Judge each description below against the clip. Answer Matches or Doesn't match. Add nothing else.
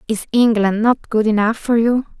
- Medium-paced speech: Matches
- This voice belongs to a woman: Matches